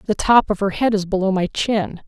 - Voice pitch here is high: Yes, high, 200 Hz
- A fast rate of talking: Yes, fast, 260 wpm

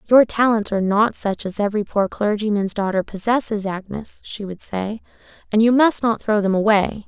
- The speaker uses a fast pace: No, average, 185 wpm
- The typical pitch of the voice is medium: No, high, 210 Hz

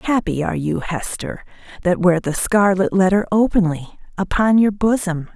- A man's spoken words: No, female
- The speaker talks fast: No, average, 145 wpm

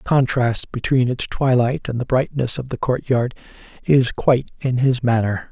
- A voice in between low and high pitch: No, low, 125 Hz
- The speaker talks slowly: No, average, 175 wpm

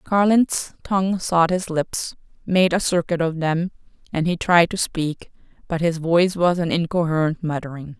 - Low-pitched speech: No, medium, 170 Hz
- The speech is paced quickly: No, average, 160 wpm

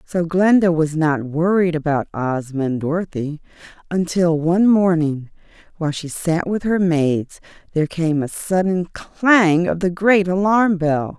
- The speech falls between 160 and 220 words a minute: No, average, 150 wpm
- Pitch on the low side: No, medium, 170 Hz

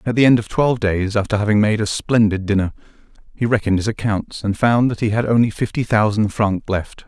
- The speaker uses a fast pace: Yes, fast, 220 wpm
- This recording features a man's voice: Yes, male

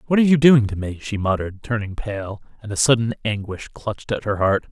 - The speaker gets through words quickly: Yes, fast, 230 wpm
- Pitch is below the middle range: Yes, low, 110 Hz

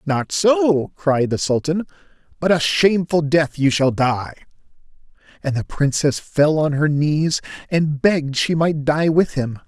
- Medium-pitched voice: Yes, medium, 150 Hz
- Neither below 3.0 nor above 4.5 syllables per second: Yes, 4.1 syllables/s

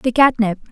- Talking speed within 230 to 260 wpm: Yes, fast, 250 wpm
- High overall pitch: Yes, high, 235 Hz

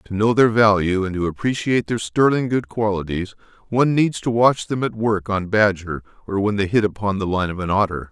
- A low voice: Yes, low, 105 Hz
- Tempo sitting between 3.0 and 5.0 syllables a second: No, 5.5 syllables/s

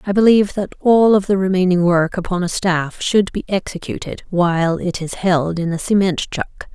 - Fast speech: No, average, 195 wpm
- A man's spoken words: No, female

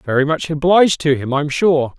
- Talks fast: Yes, fast, 210 wpm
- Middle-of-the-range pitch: Yes, medium, 150 Hz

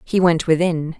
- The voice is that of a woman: Yes, female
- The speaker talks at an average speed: Yes, average, 180 wpm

